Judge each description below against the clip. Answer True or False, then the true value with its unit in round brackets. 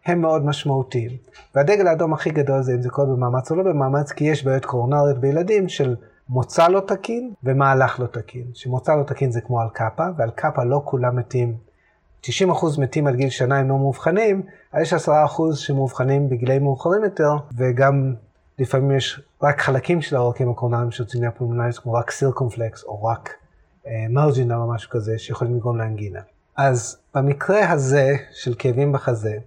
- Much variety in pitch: False (3.3 semitones)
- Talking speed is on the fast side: True (170 wpm)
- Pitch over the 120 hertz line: True (135 Hz)